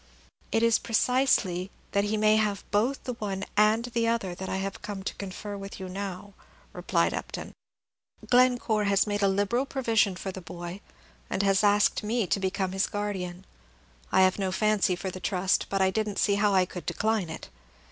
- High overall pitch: Yes, high, 200 Hz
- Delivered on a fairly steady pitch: Yes, narrow, 2.2 semitones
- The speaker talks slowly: No, average, 190 wpm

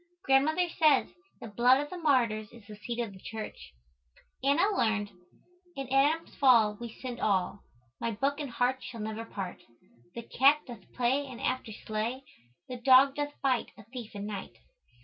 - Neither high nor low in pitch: No, high, 245 Hz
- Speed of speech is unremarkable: Yes, average, 170 wpm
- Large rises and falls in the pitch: No, average, 3.9 semitones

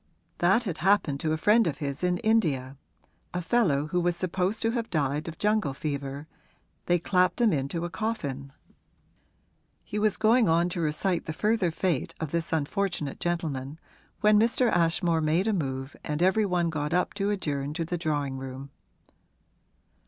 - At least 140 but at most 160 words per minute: No, average, 170 wpm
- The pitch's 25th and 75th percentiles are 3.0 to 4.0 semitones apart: No, average, 5.2 semitones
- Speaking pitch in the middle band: Yes, medium, 170 Hz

